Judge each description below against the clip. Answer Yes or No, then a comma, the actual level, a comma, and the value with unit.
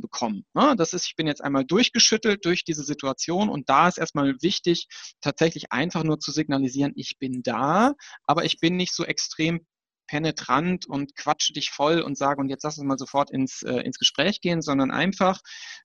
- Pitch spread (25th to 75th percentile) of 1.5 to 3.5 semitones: No, average, 4.3 semitones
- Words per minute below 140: No, fast, 190 wpm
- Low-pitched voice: No, medium, 160 Hz